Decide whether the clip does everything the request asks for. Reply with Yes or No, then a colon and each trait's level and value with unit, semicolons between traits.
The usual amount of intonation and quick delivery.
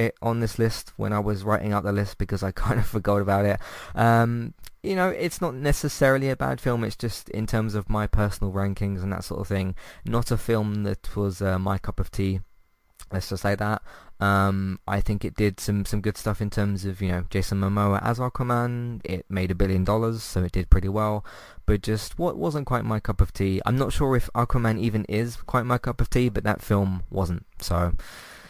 Yes: average, 3.0 semitones; fast, 225 wpm